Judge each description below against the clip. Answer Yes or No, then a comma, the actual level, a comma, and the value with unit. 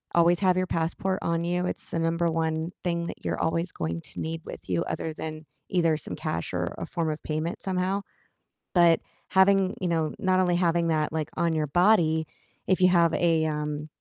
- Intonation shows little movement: Yes, narrow, 2.1 semitones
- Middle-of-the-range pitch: Yes, medium, 165 Hz